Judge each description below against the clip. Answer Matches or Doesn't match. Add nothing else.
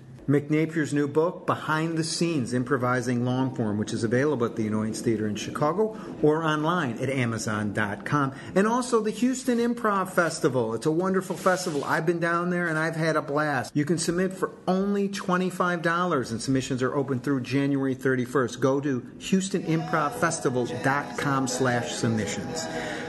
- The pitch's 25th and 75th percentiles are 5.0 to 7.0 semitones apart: Matches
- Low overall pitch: Doesn't match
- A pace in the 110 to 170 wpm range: Matches